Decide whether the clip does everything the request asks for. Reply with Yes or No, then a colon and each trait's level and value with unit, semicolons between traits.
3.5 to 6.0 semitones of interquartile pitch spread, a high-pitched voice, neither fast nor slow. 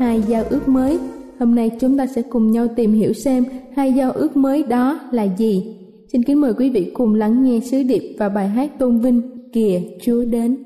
No: average, 2.8 semitones; high, 245 Hz; average, 220 wpm